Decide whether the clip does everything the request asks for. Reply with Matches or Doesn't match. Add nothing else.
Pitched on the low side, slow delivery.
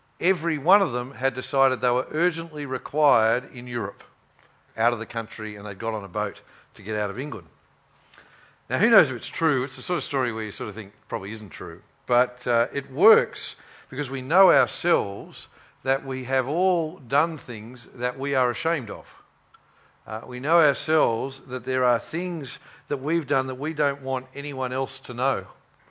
Doesn't match